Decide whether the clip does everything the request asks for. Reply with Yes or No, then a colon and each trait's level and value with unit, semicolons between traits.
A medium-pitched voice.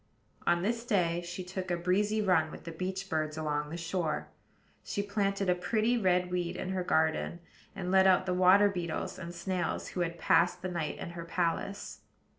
Yes: medium, 180 Hz